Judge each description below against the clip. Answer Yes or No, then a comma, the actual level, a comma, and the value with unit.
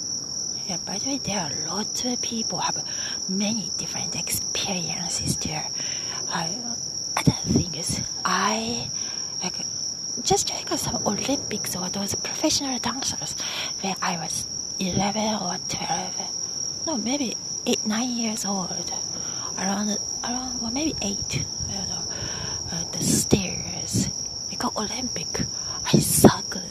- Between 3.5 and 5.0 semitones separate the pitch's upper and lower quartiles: Yes, average, 4.4 semitones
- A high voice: Yes, high, 215 Hz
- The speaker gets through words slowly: Yes, slow, 125 wpm